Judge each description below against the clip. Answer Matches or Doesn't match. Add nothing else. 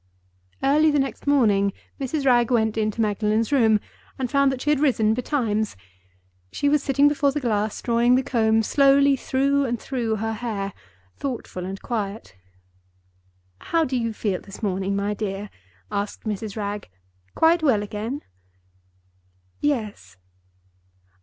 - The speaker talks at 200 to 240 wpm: Doesn't match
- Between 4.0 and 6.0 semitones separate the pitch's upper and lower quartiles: Matches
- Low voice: Doesn't match